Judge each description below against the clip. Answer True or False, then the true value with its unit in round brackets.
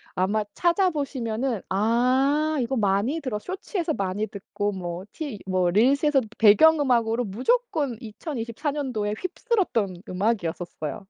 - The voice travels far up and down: True (6.4 semitones)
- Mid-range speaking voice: False (235 Hz)